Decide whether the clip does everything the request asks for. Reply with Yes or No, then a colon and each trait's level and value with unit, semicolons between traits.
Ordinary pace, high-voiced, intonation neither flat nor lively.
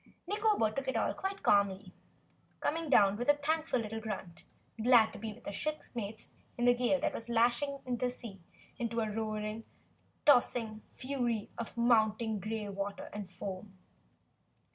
Yes: average, 155 wpm; high, 225 Hz; average, 3.1 semitones